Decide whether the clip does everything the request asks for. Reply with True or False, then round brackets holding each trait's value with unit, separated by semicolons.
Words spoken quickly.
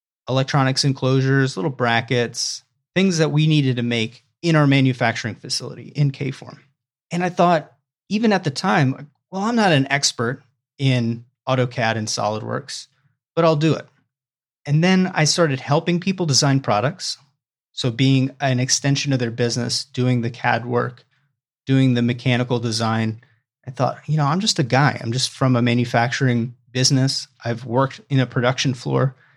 False (165 wpm)